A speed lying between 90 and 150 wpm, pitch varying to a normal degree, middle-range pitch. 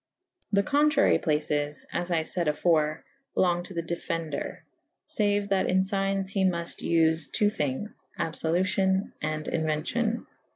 Yes: average, 140 wpm; average, 3.7 semitones; medium, 175 Hz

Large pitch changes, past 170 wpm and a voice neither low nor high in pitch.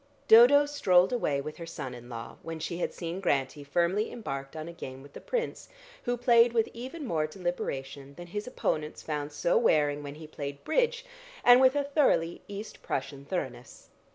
Yes: wide, 8.6 semitones; average, 185 wpm; medium, 170 Hz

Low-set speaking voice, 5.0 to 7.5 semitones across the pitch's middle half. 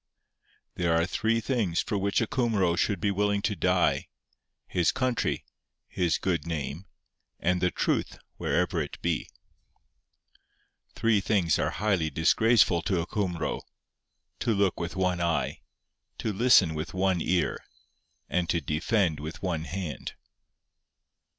No: very low, 90 Hz; average, 3.5 semitones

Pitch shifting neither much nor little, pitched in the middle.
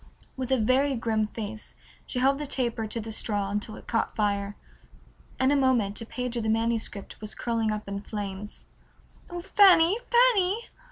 No: average, 4.1 semitones; high, 230 Hz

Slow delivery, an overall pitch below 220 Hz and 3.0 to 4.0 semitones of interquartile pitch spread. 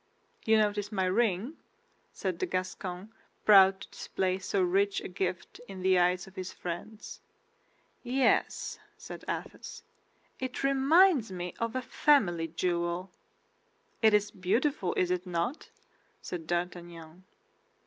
Yes: slow, 130 wpm; high, 190 Hz; average, 3.6 semitones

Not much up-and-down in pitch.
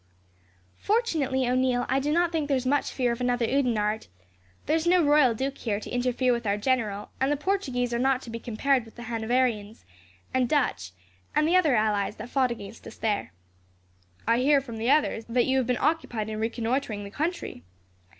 No: average, 3.6 semitones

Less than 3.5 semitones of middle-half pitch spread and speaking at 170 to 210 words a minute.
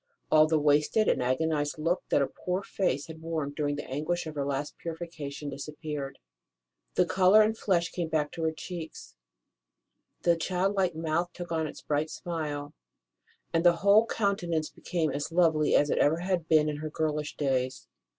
Yes: average, 2.8 semitones; average, 175 wpm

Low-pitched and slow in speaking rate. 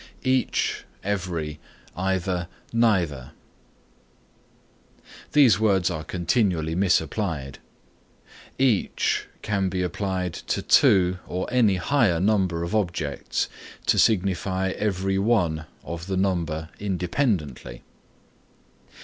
Yes: very low, 95 Hz; slow, 90 wpm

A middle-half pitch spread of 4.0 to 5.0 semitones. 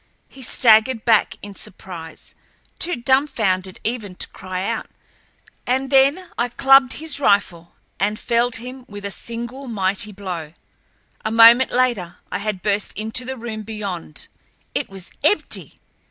Yes: average, 4.5 semitones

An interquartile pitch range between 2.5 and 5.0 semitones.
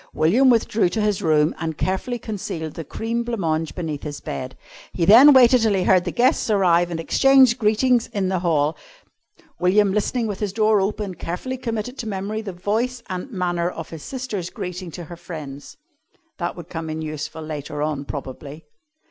No: wide, 5.5 semitones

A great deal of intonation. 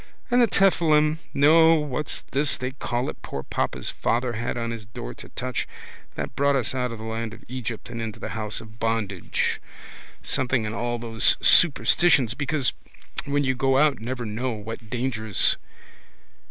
No: average, 3.9 semitones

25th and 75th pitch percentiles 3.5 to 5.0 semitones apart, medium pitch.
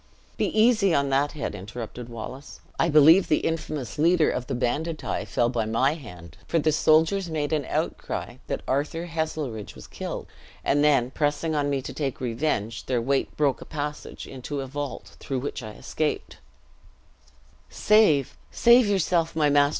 Yes: average, 4.0 semitones; medium, 145 Hz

